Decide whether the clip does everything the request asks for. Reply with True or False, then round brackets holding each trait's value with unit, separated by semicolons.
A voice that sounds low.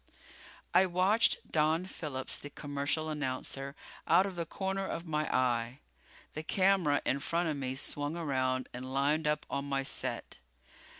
False (150 Hz)